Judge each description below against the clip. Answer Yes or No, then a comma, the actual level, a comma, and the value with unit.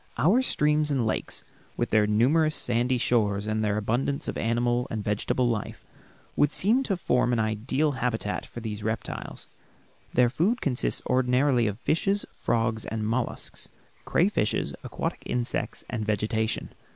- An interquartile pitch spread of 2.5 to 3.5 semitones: No, average, 4.3 semitones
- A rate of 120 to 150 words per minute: Yes, average, 145 wpm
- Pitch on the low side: Yes, low, 120 Hz